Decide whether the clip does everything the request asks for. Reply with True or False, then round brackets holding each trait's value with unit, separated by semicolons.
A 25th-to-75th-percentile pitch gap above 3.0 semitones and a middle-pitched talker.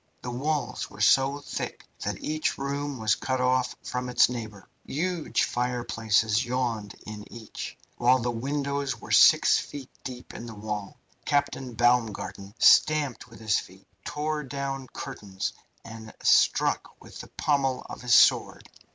False (3.7 semitones; 125 Hz)